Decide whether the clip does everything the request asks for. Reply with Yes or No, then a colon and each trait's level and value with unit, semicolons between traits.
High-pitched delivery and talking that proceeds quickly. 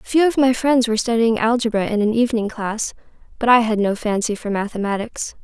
Yes: high, 225 Hz; fast, 210 wpm